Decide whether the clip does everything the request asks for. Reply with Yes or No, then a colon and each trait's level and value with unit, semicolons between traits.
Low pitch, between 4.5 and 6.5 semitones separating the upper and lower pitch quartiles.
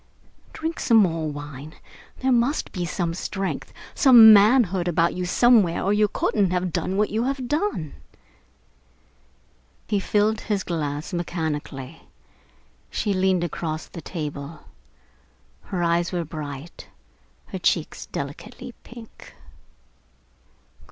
No: medium, 180 Hz; average, 4.8 semitones